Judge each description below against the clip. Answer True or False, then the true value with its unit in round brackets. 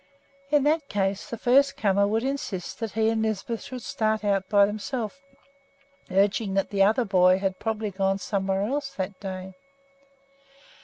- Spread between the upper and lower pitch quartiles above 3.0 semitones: False (2.7 semitones)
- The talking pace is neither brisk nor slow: True (160 wpm)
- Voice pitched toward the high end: True (205 Hz)